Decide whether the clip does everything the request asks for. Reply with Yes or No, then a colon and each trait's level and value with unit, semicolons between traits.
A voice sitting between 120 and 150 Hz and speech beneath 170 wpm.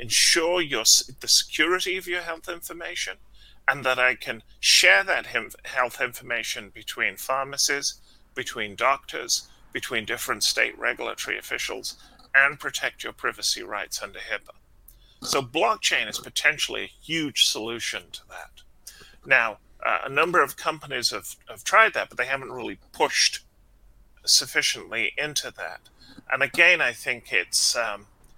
Yes: medium, 140 Hz; average, 140 wpm